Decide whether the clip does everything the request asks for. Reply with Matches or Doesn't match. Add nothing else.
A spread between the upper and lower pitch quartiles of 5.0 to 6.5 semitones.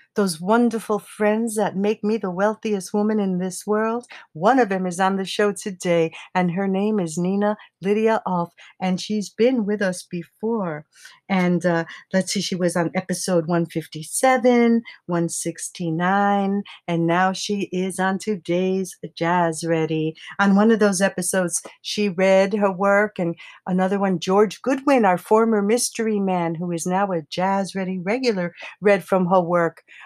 Doesn't match